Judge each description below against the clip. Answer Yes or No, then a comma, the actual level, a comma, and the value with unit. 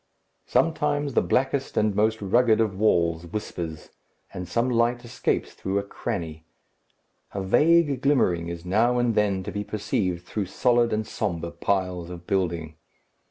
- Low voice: Yes, low, 105 Hz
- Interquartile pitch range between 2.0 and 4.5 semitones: No, average, 5.3 semitones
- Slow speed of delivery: No, average, 150 wpm